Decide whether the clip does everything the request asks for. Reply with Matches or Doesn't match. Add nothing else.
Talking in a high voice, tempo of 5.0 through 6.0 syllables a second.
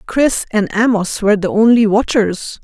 Doesn't match